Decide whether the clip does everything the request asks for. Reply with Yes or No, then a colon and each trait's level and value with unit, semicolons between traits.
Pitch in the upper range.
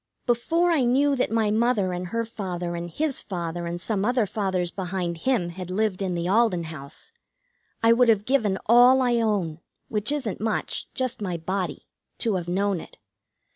Yes: high, 205 Hz